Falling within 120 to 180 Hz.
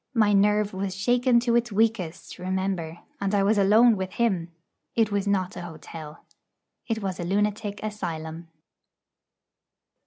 No: high, 200 Hz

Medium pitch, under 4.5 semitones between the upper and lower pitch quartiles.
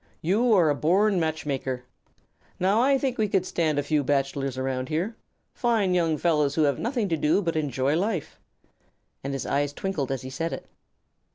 No: medium, 160 Hz; wide, 5.5 semitones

